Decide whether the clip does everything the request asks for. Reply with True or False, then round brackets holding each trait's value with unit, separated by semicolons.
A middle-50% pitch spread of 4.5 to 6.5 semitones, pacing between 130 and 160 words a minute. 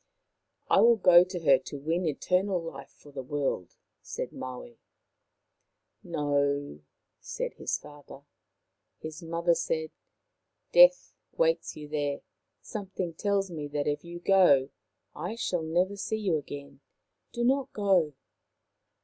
True (4.9 semitones; 140 wpm)